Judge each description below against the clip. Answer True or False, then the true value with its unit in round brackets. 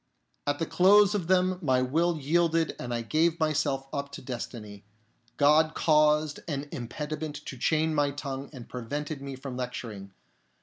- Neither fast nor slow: True (160 wpm)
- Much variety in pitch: False (3.4 semitones)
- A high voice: False (145 Hz)